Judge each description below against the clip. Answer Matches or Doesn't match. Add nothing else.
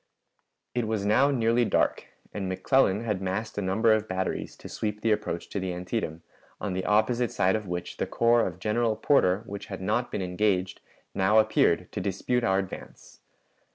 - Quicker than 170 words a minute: Matches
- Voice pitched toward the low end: Matches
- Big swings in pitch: Doesn't match